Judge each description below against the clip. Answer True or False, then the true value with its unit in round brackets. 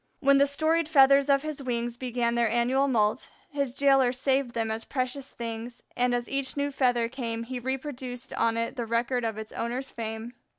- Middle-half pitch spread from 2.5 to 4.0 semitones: True (2.8 semitones)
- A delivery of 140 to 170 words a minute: False (195 wpm)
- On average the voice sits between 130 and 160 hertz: False (250 Hz)